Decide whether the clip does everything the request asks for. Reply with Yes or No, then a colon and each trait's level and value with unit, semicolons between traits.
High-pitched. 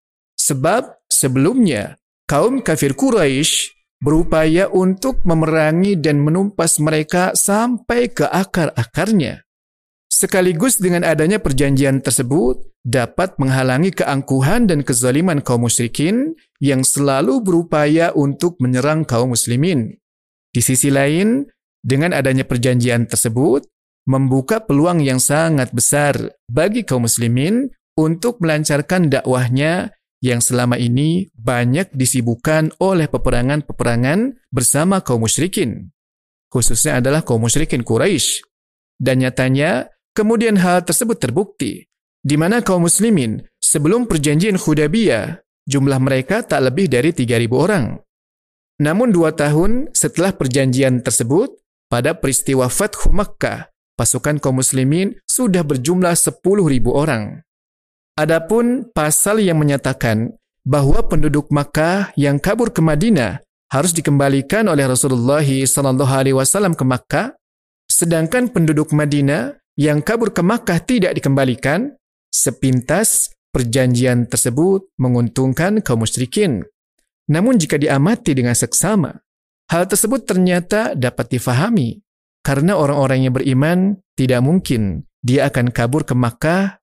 No: medium, 150 Hz